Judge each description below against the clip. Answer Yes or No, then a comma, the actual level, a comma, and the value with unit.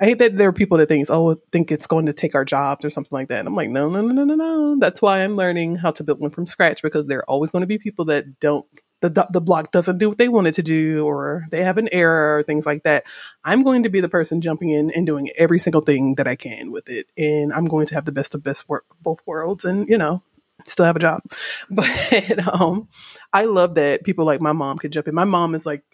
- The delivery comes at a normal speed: No, fast, 280 wpm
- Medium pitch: Yes, medium, 160 Hz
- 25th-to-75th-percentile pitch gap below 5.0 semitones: Yes, average, 3.6 semitones